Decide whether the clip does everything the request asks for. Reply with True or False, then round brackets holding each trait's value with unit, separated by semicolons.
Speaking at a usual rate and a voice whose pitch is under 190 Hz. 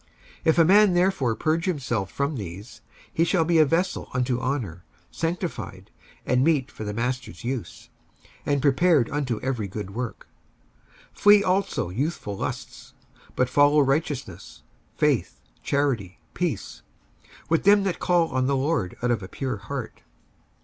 True (150 wpm; 135 Hz)